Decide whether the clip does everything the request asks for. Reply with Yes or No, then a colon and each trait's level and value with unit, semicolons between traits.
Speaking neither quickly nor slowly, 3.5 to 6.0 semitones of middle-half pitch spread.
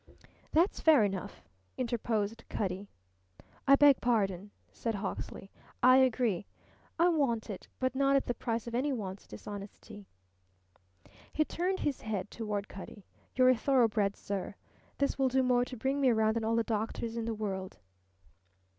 Yes: average, 155 wpm; average, 4.1 semitones